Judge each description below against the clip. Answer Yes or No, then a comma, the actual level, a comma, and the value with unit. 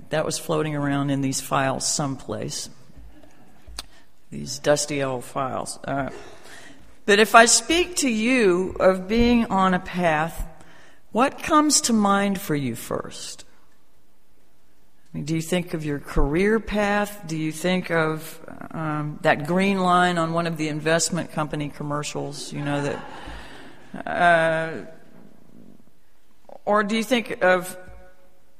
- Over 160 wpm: No, slow, 135 wpm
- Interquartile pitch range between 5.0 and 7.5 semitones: Yes, average, 5.3 semitones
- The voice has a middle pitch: Yes, medium, 165 Hz